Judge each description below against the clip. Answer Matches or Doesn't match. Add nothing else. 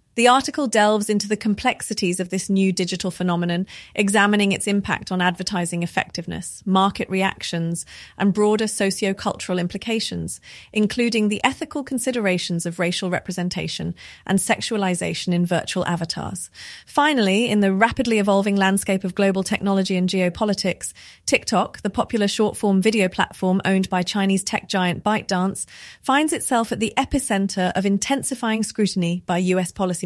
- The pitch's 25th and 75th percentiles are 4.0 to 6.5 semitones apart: Doesn't match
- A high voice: Matches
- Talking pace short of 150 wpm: Matches